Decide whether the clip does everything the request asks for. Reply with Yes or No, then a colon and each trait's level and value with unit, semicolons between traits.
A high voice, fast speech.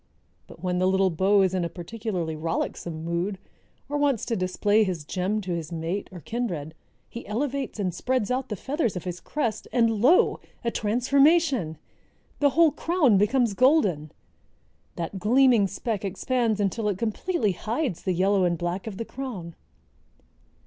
No: high, 205 Hz; average, 165 wpm